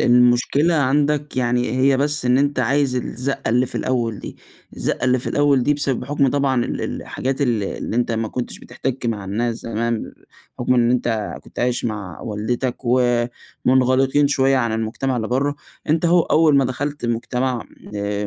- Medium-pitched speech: No, low, 125 Hz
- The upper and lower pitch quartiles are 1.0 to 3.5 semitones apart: Yes, average, 2.8 semitones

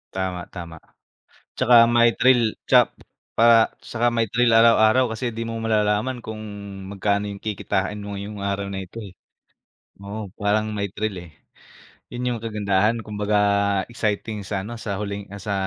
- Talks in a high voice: No, low, 105 Hz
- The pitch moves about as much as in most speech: No, narrow, 2.2 semitones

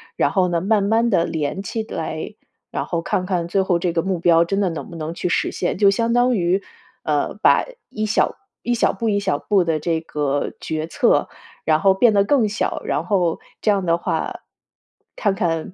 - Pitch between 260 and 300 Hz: No, medium, 185 Hz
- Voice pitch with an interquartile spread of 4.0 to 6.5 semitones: No, average, 3.3 semitones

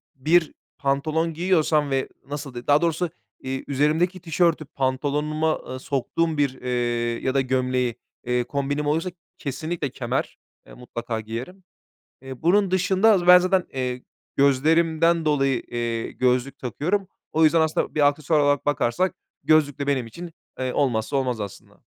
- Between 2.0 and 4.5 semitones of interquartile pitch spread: Yes, average, 4.1 semitones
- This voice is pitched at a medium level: Yes, medium, 145 Hz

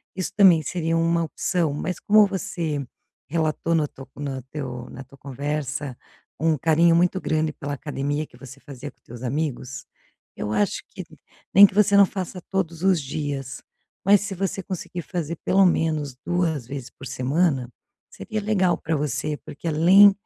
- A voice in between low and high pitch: Yes, medium, 155 Hz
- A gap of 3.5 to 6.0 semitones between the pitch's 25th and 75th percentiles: Yes, average, 4.4 semitones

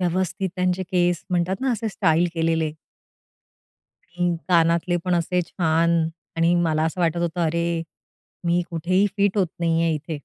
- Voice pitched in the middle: Yes, medium, 170 Hz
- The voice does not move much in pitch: Yes, narrow, 1.7 semitones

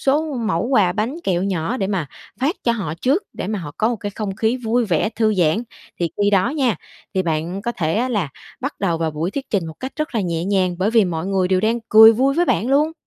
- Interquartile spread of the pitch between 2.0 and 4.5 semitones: No, average, 5.1 semitones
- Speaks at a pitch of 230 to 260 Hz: No, high, 205 Hz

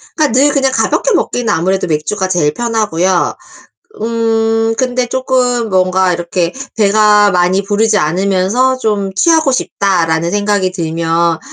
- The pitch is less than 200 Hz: No, high, 205 Hz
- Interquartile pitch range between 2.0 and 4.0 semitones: No, average, 4.4 semitones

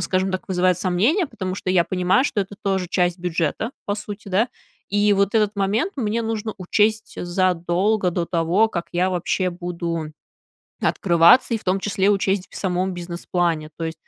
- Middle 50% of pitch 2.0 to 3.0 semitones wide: Yes, average, 2.7 semitones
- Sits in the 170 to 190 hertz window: Yes, medium, 185 Hz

